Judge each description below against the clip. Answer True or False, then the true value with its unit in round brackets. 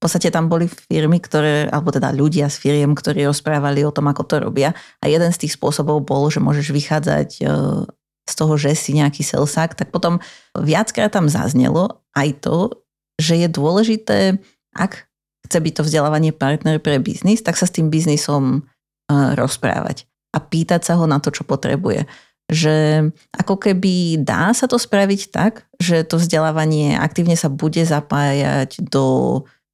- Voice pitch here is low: False (155 Hz)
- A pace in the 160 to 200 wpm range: True (165 wpm)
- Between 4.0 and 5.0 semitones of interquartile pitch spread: False (2.9 semitones)